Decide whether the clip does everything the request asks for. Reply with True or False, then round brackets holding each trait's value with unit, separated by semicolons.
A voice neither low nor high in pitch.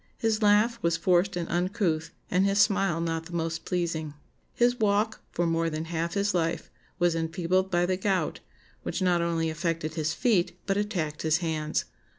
True (175 Hz)